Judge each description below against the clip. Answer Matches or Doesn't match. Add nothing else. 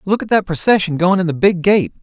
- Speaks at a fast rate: Matches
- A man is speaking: Matches